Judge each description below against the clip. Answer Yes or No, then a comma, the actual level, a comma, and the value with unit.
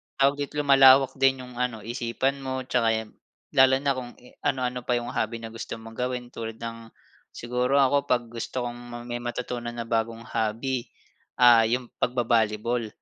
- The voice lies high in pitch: No, low, 120 Hz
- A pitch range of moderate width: No, narrow, 2.1 semitones